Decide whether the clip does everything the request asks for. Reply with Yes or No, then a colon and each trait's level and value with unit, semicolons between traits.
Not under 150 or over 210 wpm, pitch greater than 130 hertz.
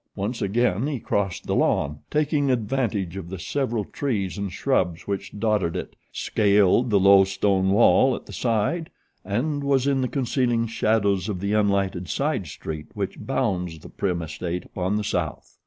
No: average, 170 wpm; low, 100 Hz